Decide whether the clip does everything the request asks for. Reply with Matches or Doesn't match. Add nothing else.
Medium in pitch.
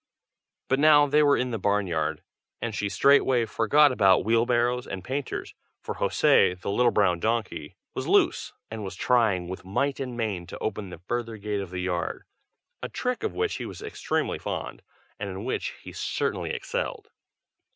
Doesn't match